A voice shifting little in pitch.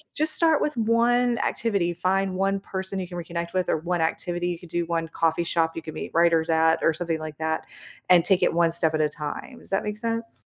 No: average, 3.2 semitones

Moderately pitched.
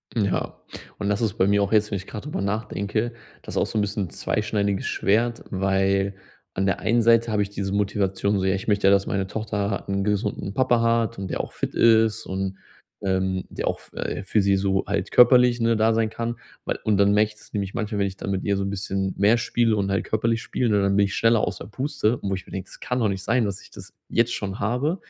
No: low, 100 Hz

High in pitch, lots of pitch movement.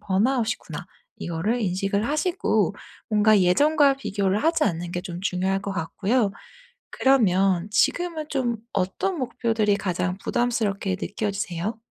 No: high, 205 Hz; average, 4.5 semitones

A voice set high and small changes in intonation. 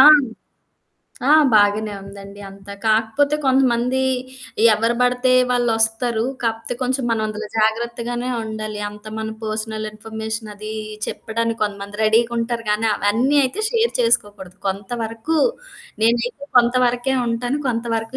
Yes: high, 225 Hz; narrow, 2.1 semitones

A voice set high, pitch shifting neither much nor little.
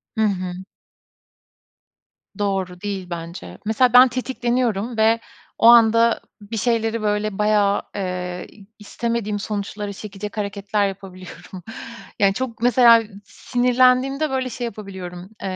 Yes: high, 210 Hz; average, 3.2 semitones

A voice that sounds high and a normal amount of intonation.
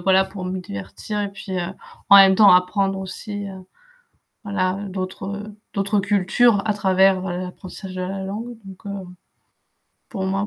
No: high, 195 Hz; narrow, 1.4 semitones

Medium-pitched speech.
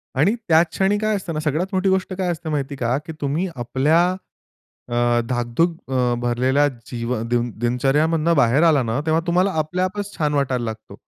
Yes: medium, 150 Hz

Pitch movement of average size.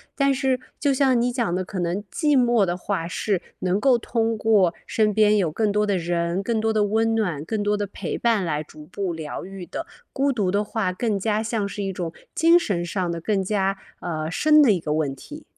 Yes: average, 4.1 semitones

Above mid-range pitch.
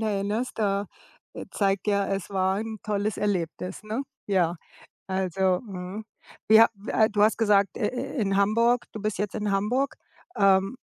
Yes: high, 205 Hz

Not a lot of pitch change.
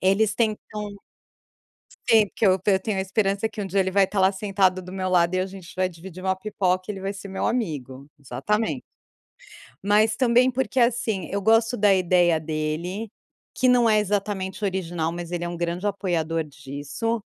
No: average, 3.2 semitones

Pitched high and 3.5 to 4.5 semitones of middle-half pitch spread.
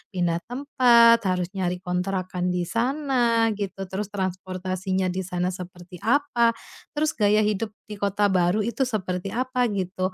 Yes: high, 195 Hz; average, 4.1 semitones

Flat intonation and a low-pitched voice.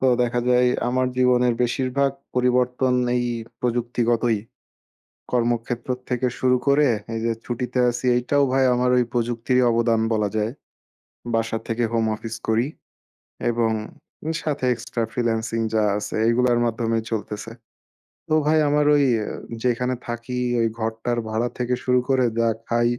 Yes: narrow, 1.7 semitones; low, 120 Hz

